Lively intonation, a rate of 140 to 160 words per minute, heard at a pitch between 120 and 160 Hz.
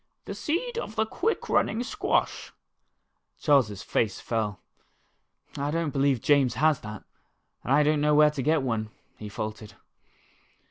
Yes: wide, 6.0 semitones; average, 150 wpm; medium, 140 Hz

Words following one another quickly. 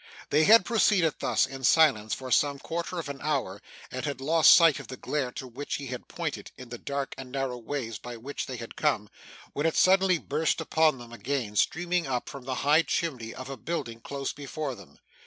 Yes: fast, 210 wpm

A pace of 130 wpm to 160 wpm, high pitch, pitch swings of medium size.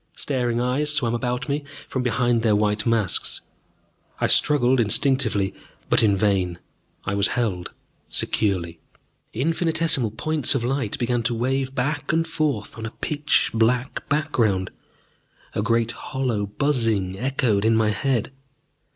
No: slow, 135 wpm; low, 120 Hz; average, 4.1 semitones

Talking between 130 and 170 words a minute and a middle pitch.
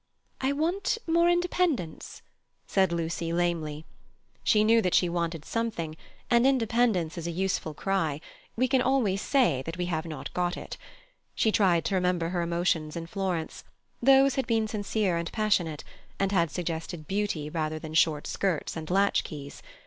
Yes: average, 165 wpm; medium, 180 Hz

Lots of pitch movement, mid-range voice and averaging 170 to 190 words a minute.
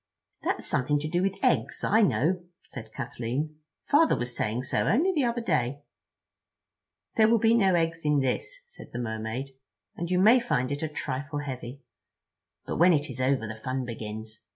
Yes: wide, 7.1 semitones; medium, 145 Hz; average, 180 wpm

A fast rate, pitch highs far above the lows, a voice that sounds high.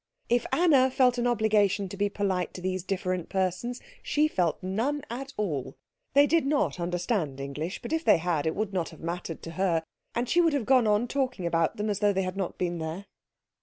Yes: fast, 215 wpm; wide, 5.9 semitones; high, 195 Hz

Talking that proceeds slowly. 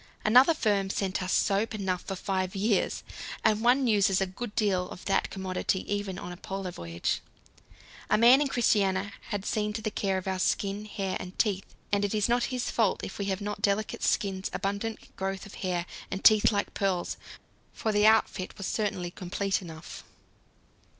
No: average, 185 wpm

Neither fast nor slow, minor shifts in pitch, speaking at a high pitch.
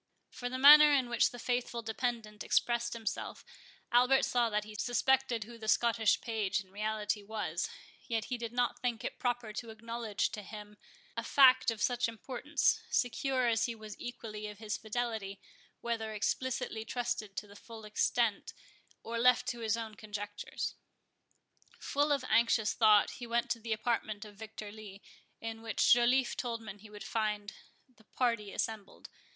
Yes: average, 170 wpm; narrow, 2.3 semitones; high, 225 Hz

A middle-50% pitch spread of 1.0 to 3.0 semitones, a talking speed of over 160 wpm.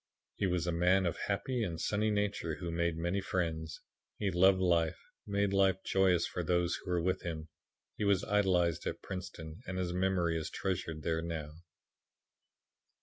Yes: narrow, 2.5 semitones; average, 175 wpm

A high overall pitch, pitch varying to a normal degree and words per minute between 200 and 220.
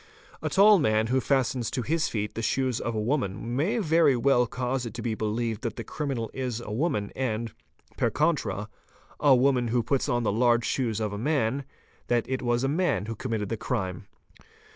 No: low, 120 Hz; average, 3.3 semitones; fast, 205 wpm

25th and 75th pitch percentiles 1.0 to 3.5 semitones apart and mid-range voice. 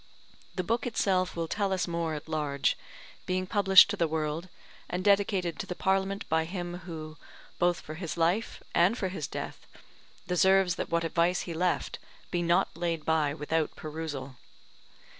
Yes: average, 2.8 semitones; medium, 175 Hz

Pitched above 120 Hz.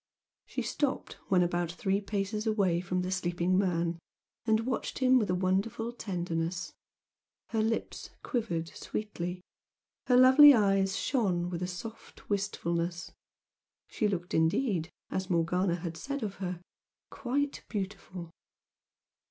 Yes: high, 190 Hz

